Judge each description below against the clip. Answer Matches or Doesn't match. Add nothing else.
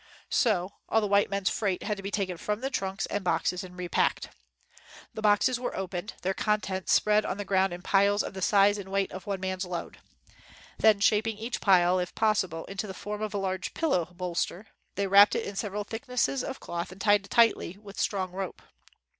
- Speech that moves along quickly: Matches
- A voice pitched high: Matches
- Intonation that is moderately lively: Doesn't match